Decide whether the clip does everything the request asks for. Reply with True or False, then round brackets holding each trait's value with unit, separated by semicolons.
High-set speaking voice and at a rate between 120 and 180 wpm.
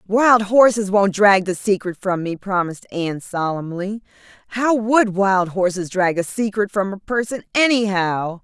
True (200 Hz; 155 wpm)